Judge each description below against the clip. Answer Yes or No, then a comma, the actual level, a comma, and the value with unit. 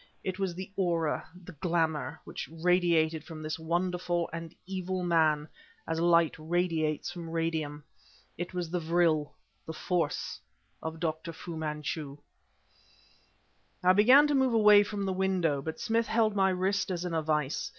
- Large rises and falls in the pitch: No, narrow, 2.6 semitones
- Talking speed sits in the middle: Yes, average, 155 wpm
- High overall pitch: No, medium, 170 Hz